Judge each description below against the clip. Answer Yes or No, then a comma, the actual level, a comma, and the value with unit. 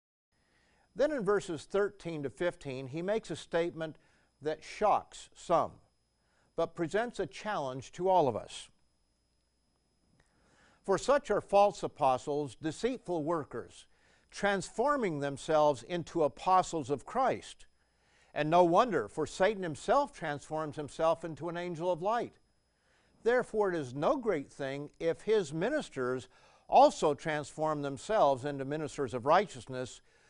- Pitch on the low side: No, medium, 160 Hz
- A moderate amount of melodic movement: Yes, average, 4.8 semitones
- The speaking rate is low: Yes, slow, 125 wpm